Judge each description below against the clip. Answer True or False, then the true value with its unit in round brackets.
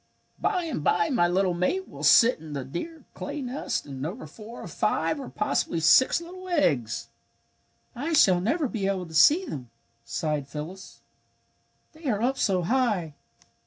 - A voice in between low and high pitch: False (195 Hz)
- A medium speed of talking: True (165 wpm)